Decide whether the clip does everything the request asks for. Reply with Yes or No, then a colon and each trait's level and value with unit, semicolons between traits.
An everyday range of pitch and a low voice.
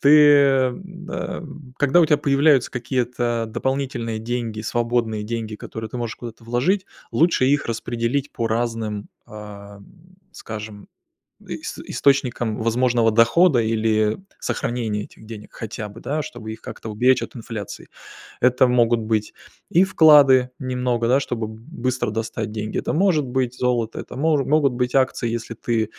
Yes: average, 3.2 semitones; low, 120 Hz